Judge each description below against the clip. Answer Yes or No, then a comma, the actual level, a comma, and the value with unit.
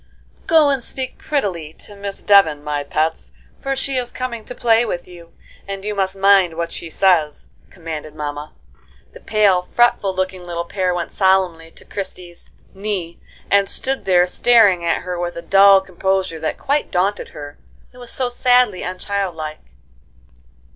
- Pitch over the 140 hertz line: Yes, high, 190 Hz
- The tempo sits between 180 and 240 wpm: No, average, 160 wpm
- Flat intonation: No, average, 3.7 semitones